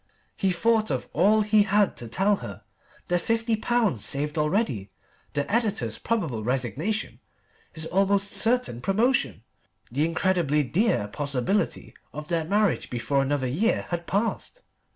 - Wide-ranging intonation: Yes, wide, 7.2 semitones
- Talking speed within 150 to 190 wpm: No, average, 140 wpm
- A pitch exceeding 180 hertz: No, medium, 175 Hz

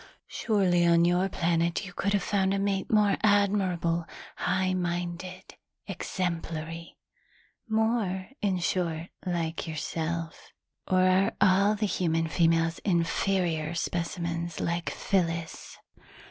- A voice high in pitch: No, medium, 175 Hz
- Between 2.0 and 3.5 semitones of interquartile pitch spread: Yes, narrow, 2.5 semitones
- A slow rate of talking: Yes, slow, 110 wpm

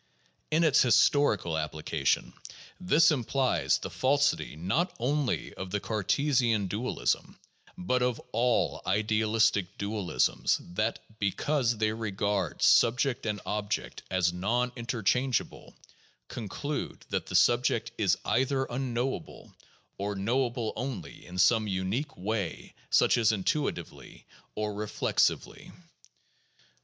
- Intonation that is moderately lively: Yes, average, 4.2 semitones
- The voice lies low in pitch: Yes, low, 110 Hz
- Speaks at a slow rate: Yes, slow, 105 wpm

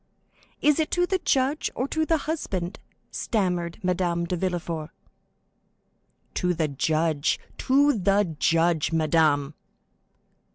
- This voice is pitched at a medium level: Yes, medium, 175 Hz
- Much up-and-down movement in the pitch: Yes, wide, 8.1 semitones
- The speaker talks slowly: Yes, slow, 110 wpm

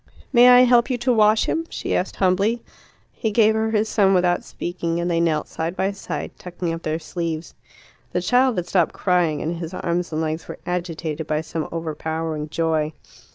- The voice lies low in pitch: No, medium, 175 Hz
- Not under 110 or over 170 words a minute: No, average, 195 wpm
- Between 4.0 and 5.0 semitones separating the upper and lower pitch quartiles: Yes, average, 4.6 semitones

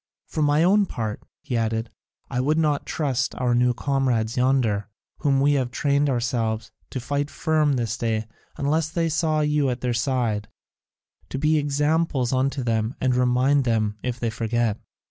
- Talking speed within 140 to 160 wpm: No, average, 170 wpm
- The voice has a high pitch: No, low, 130 Hz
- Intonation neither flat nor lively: Yes, average, 3.7 semitones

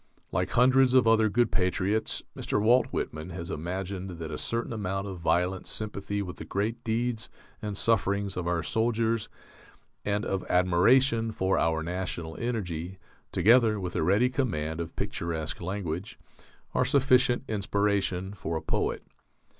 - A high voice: No, low, 100 Hz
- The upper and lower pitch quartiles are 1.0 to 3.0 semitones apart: No, average, 4.3 semitones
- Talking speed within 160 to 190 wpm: No, average, 145 wpm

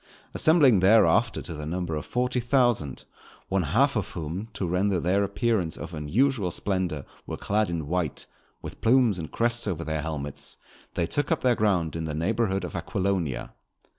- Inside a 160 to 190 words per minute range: Yes, average, 170 wpm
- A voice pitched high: No, very low, 95 Hz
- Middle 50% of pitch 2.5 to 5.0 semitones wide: No, wide, 5.6 semitones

